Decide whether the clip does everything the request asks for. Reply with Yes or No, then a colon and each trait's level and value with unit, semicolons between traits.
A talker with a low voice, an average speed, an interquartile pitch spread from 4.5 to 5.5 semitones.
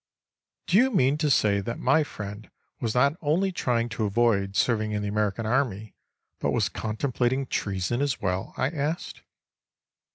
Yes: low, 120 Hz; average, 160 wpm; average, 5.2 semitones